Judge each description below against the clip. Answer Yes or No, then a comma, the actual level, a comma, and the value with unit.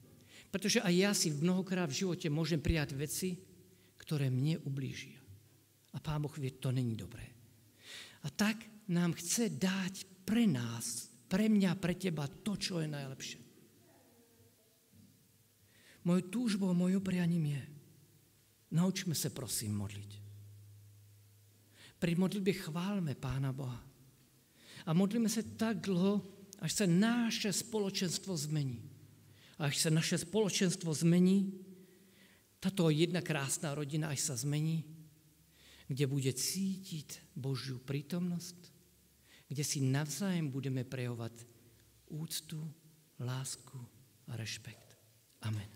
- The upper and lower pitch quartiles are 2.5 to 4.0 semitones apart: No, wide, 7.0 semitones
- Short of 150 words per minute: Yes, average, 115 wpm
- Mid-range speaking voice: Yes, medium, 150 Hz